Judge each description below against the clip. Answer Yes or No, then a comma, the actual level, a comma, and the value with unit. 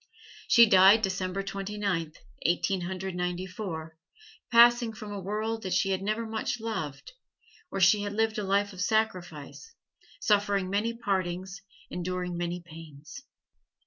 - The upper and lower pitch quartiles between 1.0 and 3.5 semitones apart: Yes, average, 3.1 semitones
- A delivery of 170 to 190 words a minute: No, average, 145 wpm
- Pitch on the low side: No, high, 195 Hz